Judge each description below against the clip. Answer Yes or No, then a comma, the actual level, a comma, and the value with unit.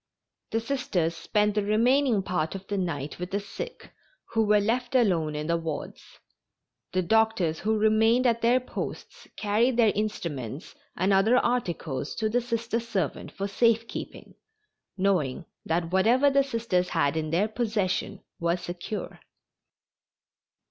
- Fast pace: No, average, 145 wpm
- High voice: Yes, high, 205 Hz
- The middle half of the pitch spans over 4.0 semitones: Yes, average, 4.8 semitones